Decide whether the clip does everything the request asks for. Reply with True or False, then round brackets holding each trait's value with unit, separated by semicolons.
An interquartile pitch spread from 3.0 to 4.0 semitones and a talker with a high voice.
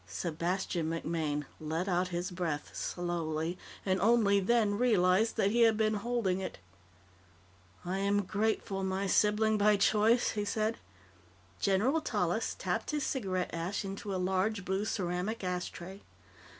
True (3.3 semitones; 195 Hz)